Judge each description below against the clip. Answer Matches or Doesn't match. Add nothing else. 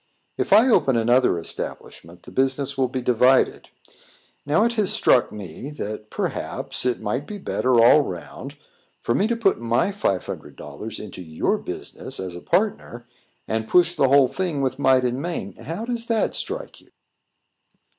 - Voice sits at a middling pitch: Doesn't match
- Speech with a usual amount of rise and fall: Doesn't match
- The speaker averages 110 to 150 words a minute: Doesn't match